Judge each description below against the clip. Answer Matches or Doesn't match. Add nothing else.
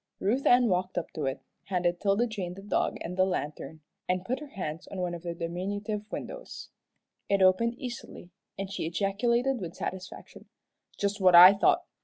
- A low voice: Doesn't match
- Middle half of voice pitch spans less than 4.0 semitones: Matches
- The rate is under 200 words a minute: Matches